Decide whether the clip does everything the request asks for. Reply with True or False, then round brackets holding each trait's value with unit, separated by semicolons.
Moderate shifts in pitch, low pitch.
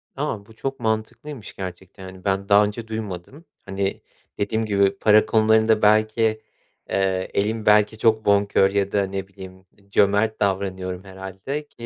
False (2.2 semitones; 100 Hz)